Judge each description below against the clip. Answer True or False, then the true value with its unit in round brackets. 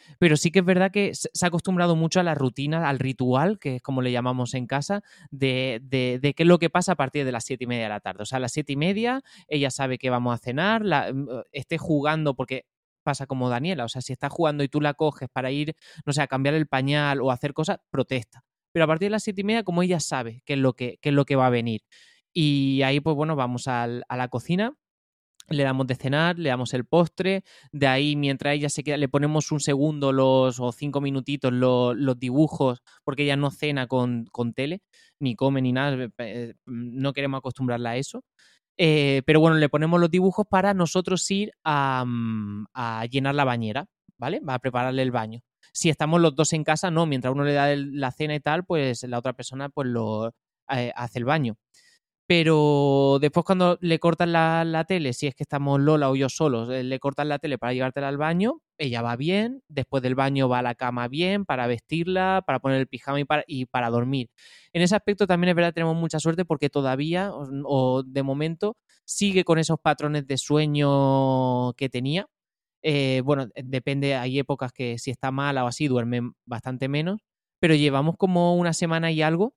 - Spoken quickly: True (220 wpm)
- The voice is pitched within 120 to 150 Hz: True (140 Hz)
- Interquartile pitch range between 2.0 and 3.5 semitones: False (3.9 semitones)